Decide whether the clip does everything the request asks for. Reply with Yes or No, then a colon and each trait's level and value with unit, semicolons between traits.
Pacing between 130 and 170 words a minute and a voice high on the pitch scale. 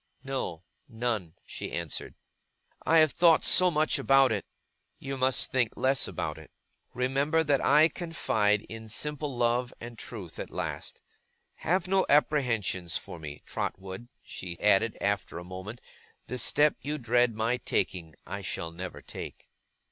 No: average, 150 wpm; low, 120 Hz